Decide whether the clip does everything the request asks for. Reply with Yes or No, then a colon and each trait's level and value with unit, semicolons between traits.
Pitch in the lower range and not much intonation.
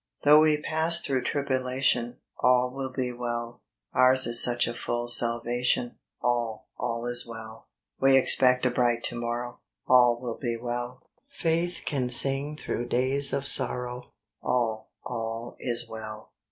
Yes: low, 125 Hz; narrow, 1.8 semitones